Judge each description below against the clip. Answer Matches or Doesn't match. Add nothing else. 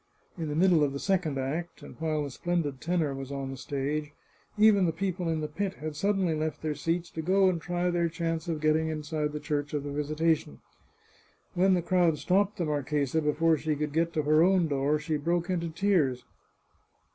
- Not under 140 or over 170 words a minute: Doesn't match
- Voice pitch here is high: Doesn't match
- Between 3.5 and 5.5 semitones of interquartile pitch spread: Doesn't match